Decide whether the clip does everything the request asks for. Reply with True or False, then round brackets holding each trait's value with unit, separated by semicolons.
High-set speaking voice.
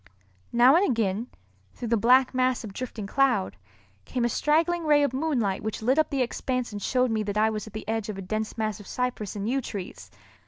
True (235 Hz)